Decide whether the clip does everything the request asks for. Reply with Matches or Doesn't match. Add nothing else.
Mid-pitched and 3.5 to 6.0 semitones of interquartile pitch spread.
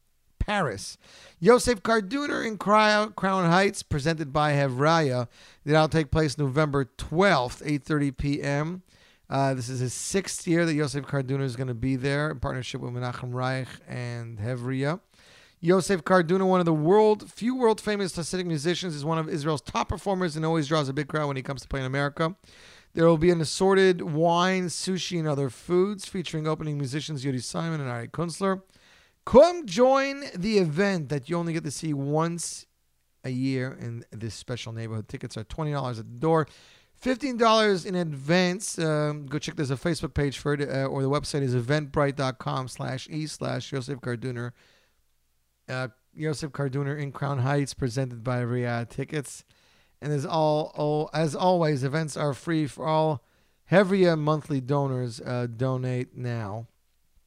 Matches